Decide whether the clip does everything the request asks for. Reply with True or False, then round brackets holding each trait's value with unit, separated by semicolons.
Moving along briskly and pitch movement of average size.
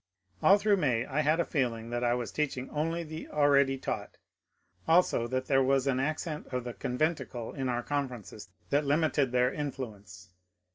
False (175 wpm; 3.5 semitones)